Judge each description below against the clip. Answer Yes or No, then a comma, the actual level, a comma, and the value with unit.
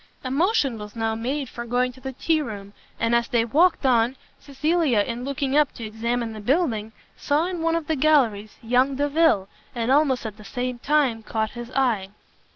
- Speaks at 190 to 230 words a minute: Yes, average, 195 wpm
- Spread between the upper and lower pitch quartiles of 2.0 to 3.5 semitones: No, average, 4.3 semitones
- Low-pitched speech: No, very high, 250 Hz